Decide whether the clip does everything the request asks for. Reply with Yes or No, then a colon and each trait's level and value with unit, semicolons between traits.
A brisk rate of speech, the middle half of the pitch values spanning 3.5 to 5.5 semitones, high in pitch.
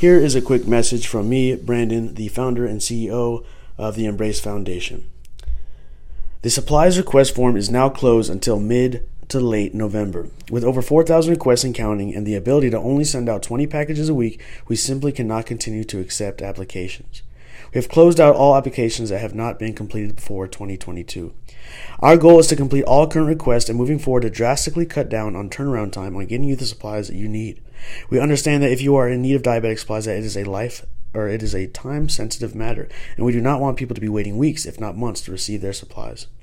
No: fast, 220 wpm; average, 3.9 semitones; low, 115 Hz